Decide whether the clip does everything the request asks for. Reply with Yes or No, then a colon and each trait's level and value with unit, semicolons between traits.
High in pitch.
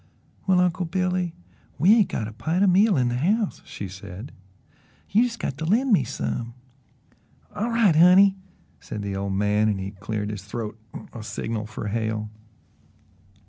No: low, 125 Hz